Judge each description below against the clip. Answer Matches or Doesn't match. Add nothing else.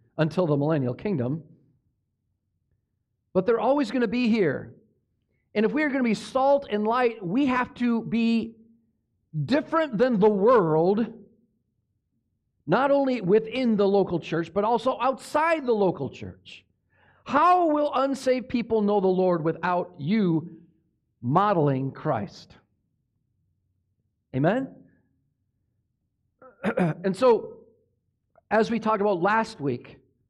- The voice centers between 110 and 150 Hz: Doesn't match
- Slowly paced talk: Matches